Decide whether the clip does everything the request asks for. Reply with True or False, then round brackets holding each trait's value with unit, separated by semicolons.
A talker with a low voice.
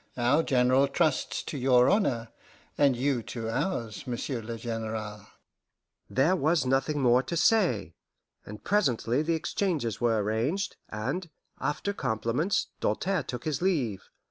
True (130 Hz)